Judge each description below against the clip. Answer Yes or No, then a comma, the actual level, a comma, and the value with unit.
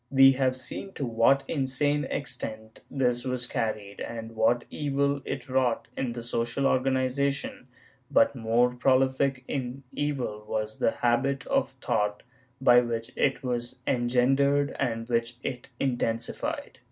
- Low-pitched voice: Yes, low, 125 Hz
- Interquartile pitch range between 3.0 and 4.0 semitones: No, narrow, 2.6 semitones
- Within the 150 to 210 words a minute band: No, slow, 135 wpm